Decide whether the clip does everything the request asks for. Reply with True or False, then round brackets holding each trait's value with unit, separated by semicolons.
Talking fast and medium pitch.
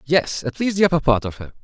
True (295 wpm; 150 Hz)